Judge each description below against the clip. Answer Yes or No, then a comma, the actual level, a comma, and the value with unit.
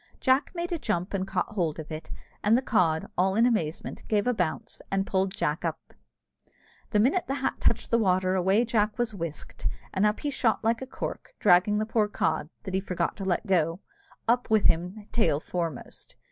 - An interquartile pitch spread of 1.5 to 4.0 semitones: No, average, 4.4 semitones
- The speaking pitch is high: Yes, high, 195 Hz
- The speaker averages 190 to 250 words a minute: Yes, average, 200 wpm